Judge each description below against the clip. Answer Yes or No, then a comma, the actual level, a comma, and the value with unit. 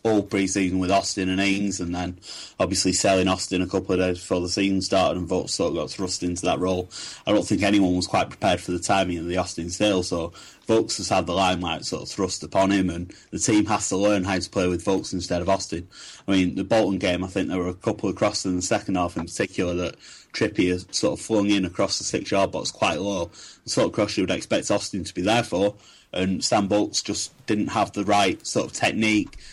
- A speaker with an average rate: No, fast, 250 wpm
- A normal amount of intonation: No, narrow, 1.8 semitones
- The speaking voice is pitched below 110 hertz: Yes, very low, 95 Hz